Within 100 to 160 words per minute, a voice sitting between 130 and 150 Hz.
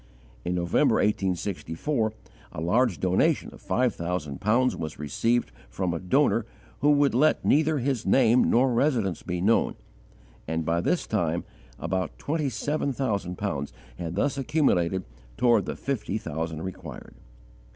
No: average, 140 wpm; low, 105 Hz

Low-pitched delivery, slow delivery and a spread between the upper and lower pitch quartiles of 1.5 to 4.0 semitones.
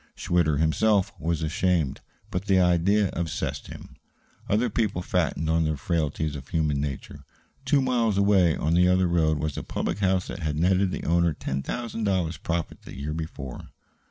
No: very low, 85 Hz; average, 175 wpm; average, 3.5 semitones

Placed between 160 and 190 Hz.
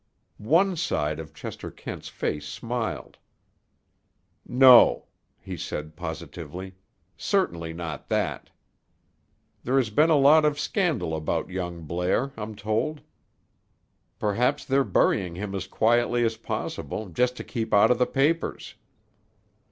No: low, 110 Hz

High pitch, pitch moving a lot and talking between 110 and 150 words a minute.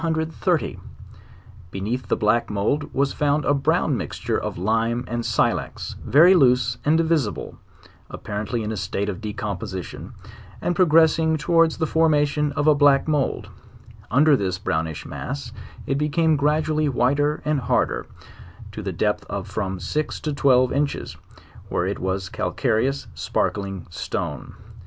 No: low, 135 Hz; wide, 6.1 semitones; average, 145 wpm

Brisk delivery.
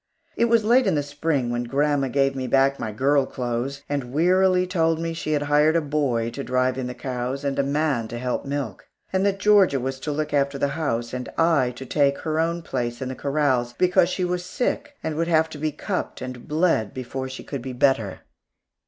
Yes: fast, 225 wpm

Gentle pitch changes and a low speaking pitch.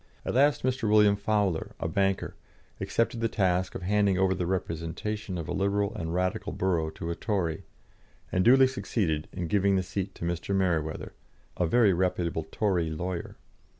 No: average, 3.4 semitones; very low, 95 Hz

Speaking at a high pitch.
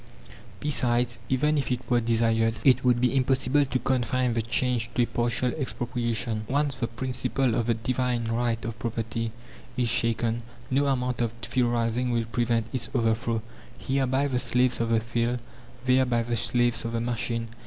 No: low, 120 Hz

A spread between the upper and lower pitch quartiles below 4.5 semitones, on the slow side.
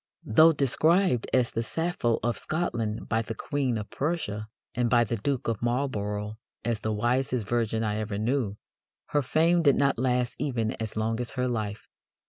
No: average, 4.0 semitones; average, 175 wpm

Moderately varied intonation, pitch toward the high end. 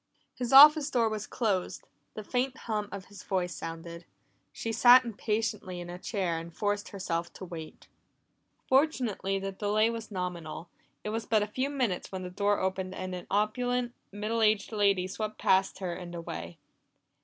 Yes: average, 3.7 semitones; high, 205 Hz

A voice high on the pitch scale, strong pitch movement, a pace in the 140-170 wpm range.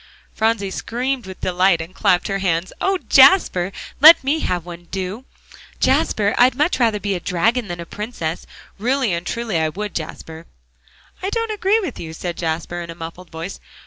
No: high, 195 Hz; wide, 6.4 semitones; average, 185 wpm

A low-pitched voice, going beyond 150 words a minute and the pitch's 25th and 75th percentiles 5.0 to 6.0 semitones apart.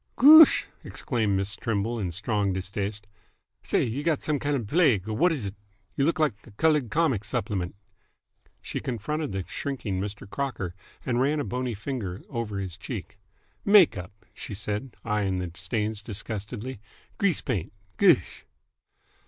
Yes: low, 110 Hz; average, 160 wpm; wide, 5.5 semitones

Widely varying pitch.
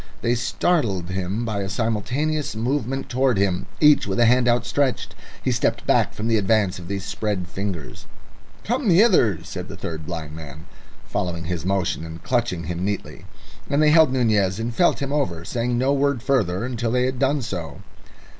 Yes: wide, 6.2 semitones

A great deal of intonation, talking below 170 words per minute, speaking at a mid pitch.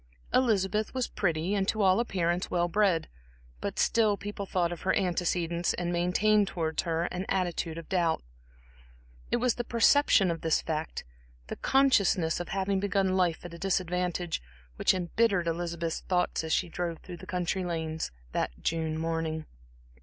No: average, 2.8 semitones; average, 160 wpm; medium, 180 Hz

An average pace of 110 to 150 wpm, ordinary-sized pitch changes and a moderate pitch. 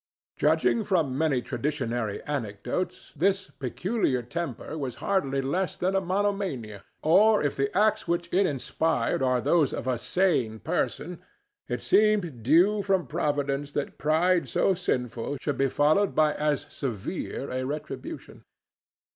No: average, 140 wpm; wide, 6.0 semitones; medium, 150 Hz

